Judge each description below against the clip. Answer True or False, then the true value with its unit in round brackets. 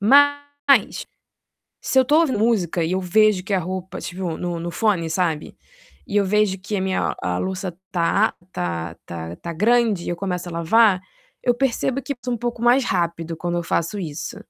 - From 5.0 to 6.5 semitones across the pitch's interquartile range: True (5.4 semitones)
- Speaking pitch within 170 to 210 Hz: True (190 Hz)